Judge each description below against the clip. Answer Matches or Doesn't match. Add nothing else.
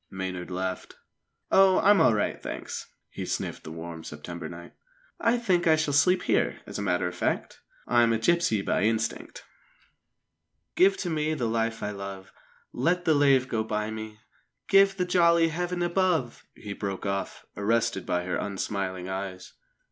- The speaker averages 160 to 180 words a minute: Matches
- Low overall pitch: Matches